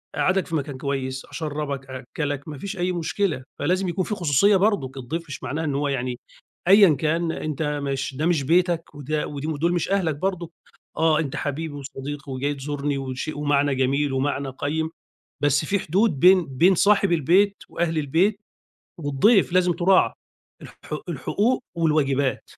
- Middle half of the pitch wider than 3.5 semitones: Yes, average, 4.0 semitones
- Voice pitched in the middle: Yes, medium, 155 Hz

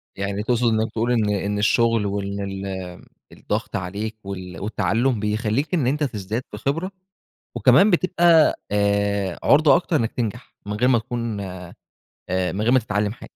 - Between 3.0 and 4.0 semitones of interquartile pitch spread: Yes, average, 3.5 semitones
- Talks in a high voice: No, low, 110 Hz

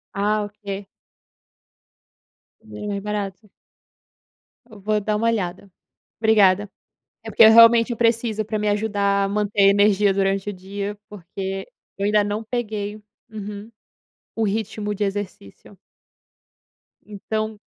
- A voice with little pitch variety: Yes, narrow, 1.5 semitones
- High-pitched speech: Yes, high, 205 Hz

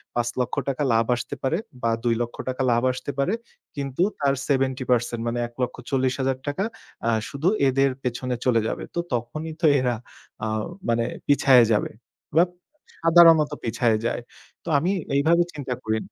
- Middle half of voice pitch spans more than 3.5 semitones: No, average, 3.2 semitones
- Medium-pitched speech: No, low, 130 Hz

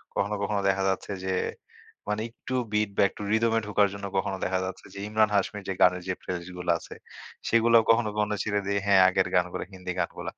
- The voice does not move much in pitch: Yes, narrow, 2.1 semitones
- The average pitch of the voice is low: Yes, low, 100 Hz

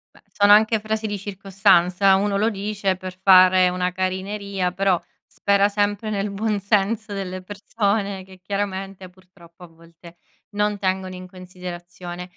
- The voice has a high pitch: Yes, high, 195 Hz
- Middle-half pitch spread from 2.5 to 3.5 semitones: No, narrow, 1.9 semitones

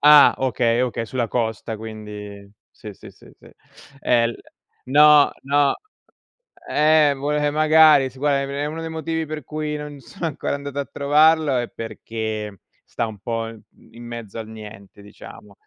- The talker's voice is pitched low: Yes, low, 130 Hz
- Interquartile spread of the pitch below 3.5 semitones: No, average, 4.9 semitones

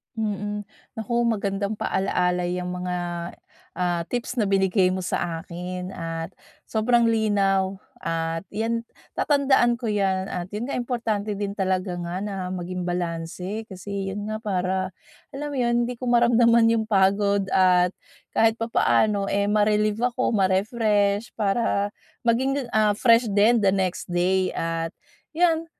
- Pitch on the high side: Yes, high, 200 Hz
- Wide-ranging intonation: No, average, 3.7 semitones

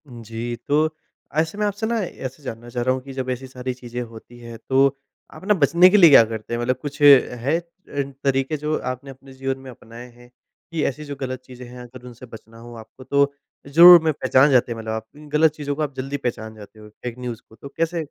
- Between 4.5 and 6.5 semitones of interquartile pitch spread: No, average, 3.3 semitones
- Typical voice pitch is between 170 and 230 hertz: No, low, 130 Hz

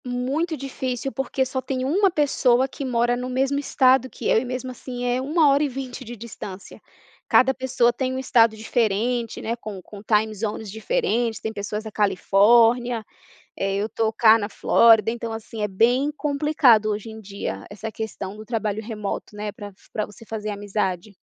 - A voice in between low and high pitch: No, high, 230 Hz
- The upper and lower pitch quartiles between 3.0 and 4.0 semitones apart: Yes, average, 3.4 semitones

